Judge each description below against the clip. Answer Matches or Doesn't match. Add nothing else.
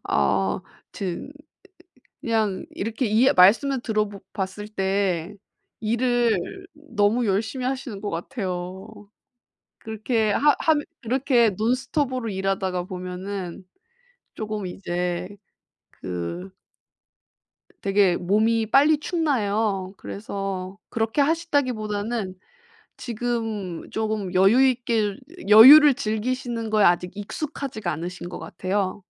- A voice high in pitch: Matches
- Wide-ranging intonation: Doesn't match